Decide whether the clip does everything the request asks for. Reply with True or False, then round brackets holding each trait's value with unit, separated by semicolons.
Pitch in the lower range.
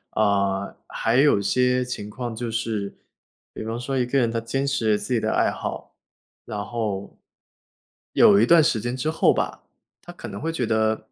True (115 Hz)